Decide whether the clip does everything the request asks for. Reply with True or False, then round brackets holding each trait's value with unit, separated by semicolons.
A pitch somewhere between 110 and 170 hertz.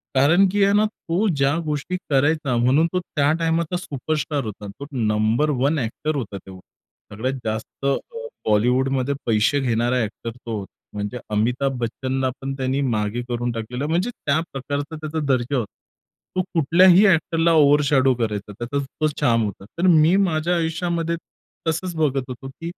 True (140 Hz)